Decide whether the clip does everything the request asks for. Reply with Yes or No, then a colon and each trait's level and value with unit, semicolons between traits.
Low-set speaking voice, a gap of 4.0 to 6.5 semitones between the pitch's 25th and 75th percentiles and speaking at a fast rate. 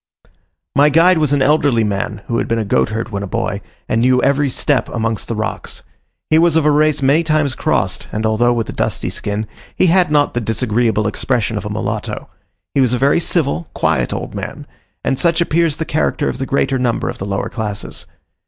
Yes: low, 130 Hz; average, 5.2 semitones; fast, 210 wpm